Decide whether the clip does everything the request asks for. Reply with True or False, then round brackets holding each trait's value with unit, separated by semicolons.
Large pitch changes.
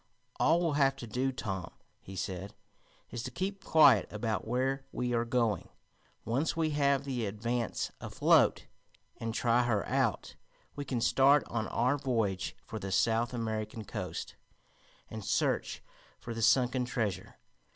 False (3.6 semitones)